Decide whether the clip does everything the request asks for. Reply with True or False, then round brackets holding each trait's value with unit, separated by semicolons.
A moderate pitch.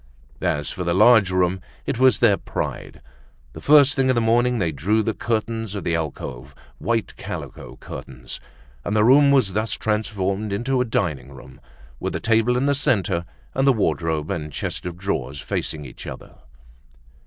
False (105 Hz)